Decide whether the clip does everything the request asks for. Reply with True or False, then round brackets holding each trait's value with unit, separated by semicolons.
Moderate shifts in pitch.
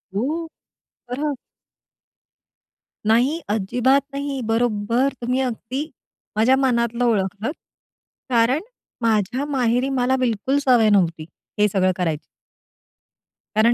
True (3.6 semitones)